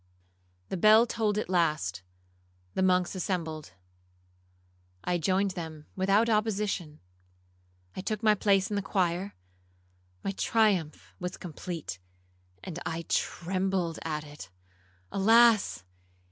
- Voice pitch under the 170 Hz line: No, medium, 175 Hz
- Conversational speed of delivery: No, slow, 100 wpm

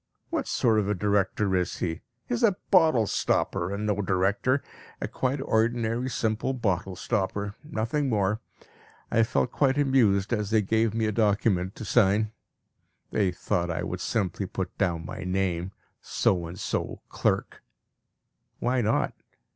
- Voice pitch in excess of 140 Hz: No, low, 105 Hz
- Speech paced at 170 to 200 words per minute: No, average, 155 wpm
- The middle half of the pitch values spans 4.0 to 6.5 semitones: No, average, 3.6 semitones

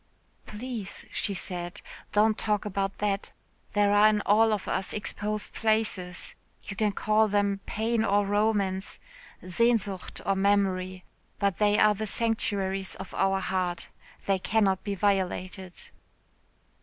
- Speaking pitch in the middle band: No, high, 200 Hz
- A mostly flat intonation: Yes, narrow, 1.9 semitones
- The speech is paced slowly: Yes, slow, 130 wpm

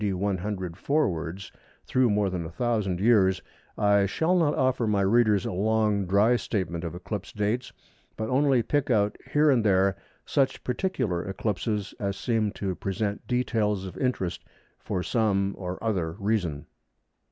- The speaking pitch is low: Yes, low, 105 Hz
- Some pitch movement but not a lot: Yes, average, 3.8 semitones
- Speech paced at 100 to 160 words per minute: Yes, average, 150 wpm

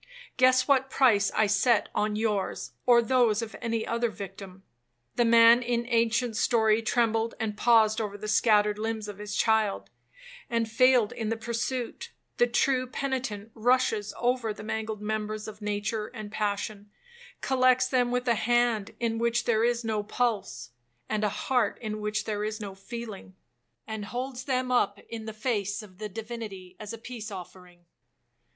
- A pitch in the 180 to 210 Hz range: No, high, 220 Hz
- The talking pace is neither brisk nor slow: Yes, average, 165 wpm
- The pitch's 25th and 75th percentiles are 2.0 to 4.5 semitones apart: Yes, narrow, 2.4 semitones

